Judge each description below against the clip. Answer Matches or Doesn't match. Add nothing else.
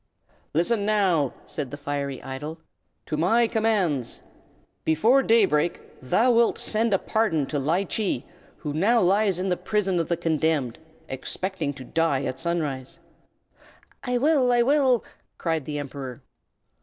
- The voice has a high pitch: Doesn't match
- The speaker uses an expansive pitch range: Matches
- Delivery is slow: Doesn't match